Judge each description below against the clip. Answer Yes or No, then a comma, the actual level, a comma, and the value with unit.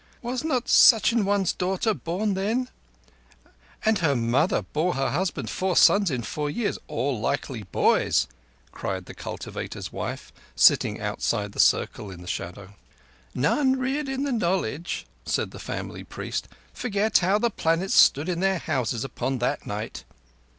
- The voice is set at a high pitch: No, medium, 180 Hz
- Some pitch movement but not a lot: No, wide, 8.5 semitones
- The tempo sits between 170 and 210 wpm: No, average, 155 wpm